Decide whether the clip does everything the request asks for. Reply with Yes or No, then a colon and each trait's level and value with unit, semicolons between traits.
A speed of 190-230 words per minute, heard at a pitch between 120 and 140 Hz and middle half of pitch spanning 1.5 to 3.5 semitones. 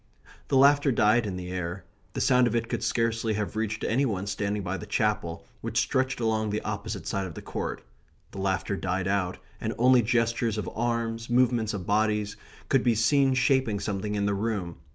No: average, 195 wpm; low, 110 Hz; average, 2.9 semitones